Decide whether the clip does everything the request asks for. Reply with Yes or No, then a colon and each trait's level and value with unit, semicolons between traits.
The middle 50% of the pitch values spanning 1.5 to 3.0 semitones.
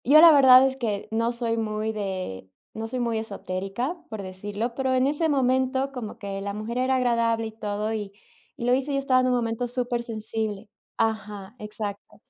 No: average, 3.4 semitones